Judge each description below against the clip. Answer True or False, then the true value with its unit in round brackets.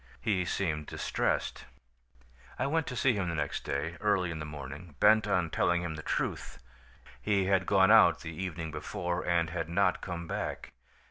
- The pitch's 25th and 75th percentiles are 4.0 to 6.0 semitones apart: False (3.5 semitones)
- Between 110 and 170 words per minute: False (180 wpm)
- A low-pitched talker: True (85 Hz)